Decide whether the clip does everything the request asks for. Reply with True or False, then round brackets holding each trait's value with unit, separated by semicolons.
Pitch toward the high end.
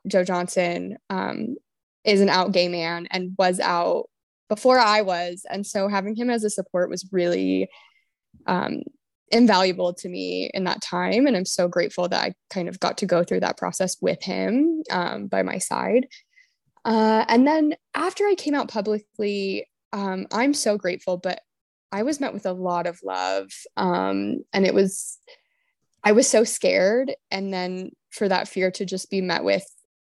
True (195 Hz)